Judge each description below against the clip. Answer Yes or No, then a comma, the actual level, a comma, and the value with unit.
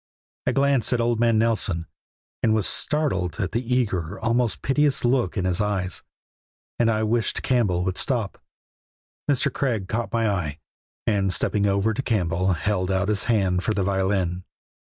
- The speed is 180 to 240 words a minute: No, average, 165 wpm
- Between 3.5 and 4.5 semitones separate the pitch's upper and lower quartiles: Yes, average, 4.0 semitones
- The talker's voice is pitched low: Yes, low, 105 Hz